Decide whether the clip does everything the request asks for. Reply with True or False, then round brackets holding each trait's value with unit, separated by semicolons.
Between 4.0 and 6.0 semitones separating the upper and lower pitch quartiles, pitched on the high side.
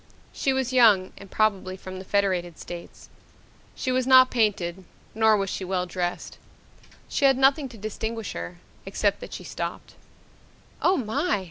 True (5.2 semitones; 205 Hz)